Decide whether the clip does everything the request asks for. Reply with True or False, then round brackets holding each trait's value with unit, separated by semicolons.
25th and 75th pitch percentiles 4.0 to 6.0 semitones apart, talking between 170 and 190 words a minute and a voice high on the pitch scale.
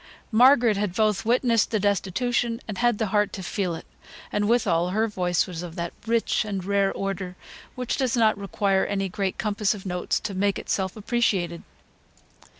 False (3.0 semitones; 175 wpm; 205 Hz)